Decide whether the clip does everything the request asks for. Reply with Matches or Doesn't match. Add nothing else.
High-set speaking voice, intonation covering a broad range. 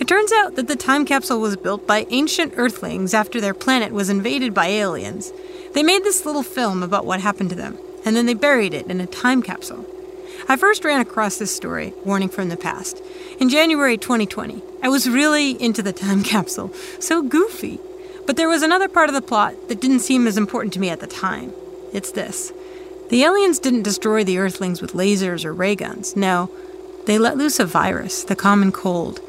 Matches